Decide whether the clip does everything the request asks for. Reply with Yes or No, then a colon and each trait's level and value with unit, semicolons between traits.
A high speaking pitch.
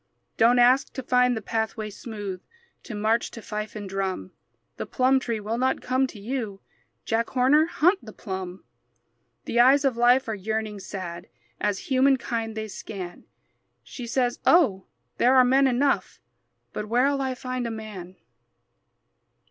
Yes: high, 230 Hz